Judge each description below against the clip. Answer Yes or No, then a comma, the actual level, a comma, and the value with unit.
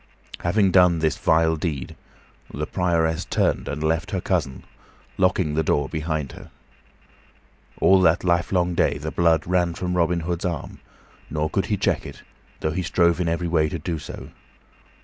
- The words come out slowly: No, average, 170 wpm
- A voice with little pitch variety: Yes, narrow, 2.2 semitones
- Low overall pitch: Yes, very low, 85 Hz